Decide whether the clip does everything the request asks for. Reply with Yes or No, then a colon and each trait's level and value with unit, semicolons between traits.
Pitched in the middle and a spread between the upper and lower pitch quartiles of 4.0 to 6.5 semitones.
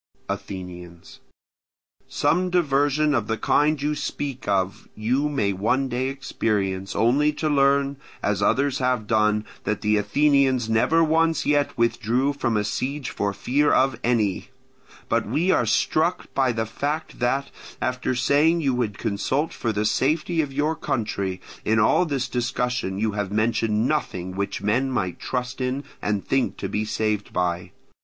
No: low, 125 Hz; average, 5.0 semitones